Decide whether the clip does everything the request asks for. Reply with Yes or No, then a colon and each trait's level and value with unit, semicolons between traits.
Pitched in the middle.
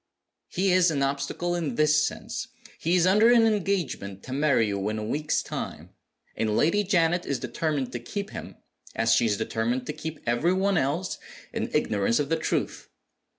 Yes: medium, 150 Hz